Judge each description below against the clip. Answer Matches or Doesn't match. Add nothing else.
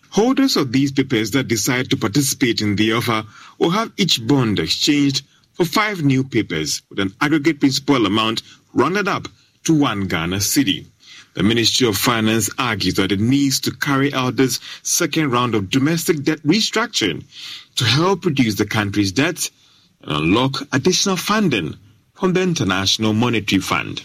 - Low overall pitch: Matches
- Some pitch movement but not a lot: Doesn't match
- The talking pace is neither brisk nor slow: Matches